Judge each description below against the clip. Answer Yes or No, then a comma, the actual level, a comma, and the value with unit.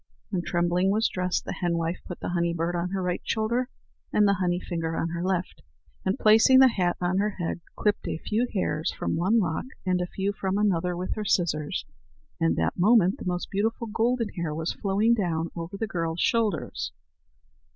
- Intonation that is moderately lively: Yes, average, 3.4 semitones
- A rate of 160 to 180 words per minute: No, average, 195 wpm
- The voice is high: No, medium, 180 Hz